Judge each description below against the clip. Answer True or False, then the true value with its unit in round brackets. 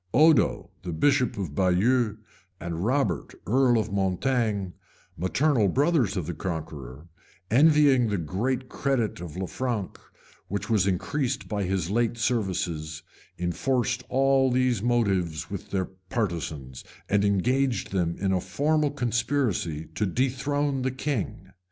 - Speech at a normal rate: False (125 wpm)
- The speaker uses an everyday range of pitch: False (6.1 semitones)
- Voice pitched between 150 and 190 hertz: False (110 Hz)